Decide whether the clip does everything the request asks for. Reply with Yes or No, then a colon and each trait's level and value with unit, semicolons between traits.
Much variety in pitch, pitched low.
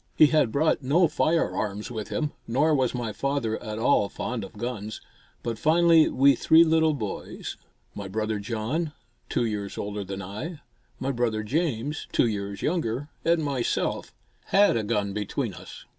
Yes: wide, 6.3 semitones; low, 120 Hz